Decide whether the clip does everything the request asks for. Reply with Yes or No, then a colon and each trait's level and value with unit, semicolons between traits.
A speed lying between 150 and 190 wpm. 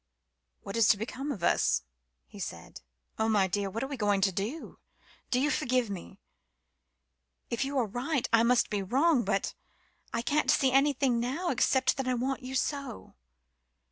Yes: average, 170 wpm